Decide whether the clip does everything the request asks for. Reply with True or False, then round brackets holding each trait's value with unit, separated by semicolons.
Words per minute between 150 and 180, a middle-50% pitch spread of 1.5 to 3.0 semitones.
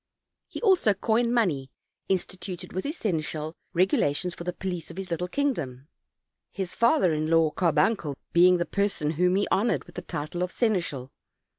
False (170 wpm; 4.0 semitones)